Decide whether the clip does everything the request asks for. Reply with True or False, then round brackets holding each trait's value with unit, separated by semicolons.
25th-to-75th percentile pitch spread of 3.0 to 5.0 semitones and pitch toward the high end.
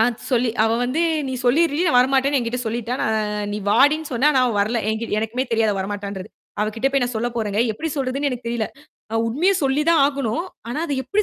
True (4.0 semitones; 245 Hz)